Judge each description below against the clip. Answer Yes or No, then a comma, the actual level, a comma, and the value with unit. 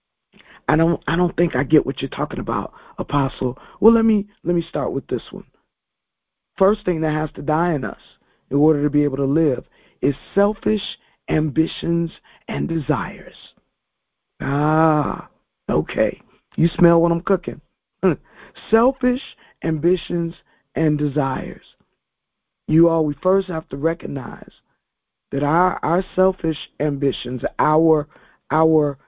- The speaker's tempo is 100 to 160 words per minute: Yes, slow, 135 wpm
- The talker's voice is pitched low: No, medium, 160 Hz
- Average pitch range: Yes, average, 3.0 semitones